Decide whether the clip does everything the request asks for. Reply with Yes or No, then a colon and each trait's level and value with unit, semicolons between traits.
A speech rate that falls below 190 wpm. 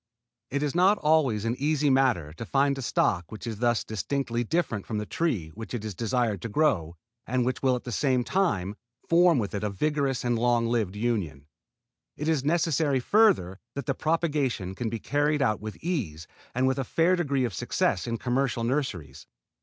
No: average, 195 wpm